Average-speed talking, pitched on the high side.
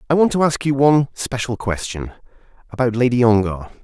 No: average, 155 wpm; low, 125 Hz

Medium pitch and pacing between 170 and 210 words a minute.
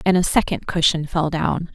Yes: medium, 165 Hz; fast, 205 wpm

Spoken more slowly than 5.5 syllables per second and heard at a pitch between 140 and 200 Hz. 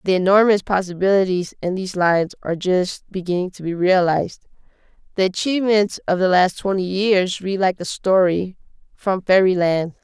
Yes: 5.3 syllables/s; medium, 185 Hz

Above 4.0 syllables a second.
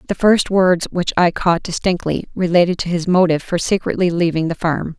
Yes: 5.4 syllables/s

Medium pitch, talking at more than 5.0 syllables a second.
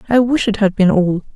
No: high, 210 Hz; 5.5 syllables/s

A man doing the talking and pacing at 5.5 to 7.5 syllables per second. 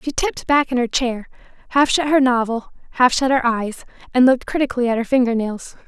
No: female; 6.0 syllables/s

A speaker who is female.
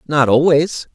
No: male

